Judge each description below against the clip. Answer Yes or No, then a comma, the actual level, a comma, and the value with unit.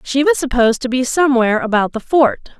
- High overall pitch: Yes, very high, 260 Hz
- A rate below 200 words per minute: No, fast, 210 wpm